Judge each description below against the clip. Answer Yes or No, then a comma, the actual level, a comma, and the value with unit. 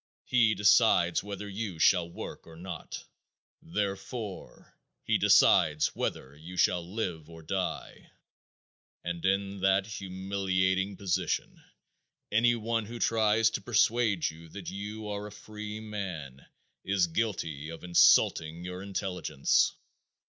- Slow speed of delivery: Yes, slow, 120 wpm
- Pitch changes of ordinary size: Yes, average, 3.4 semitones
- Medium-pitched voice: No, very low, 95 Hz